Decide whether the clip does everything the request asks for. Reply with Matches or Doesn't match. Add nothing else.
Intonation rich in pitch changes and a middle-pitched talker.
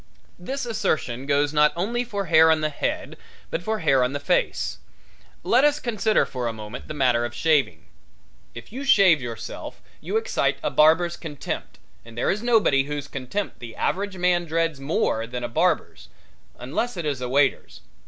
Matches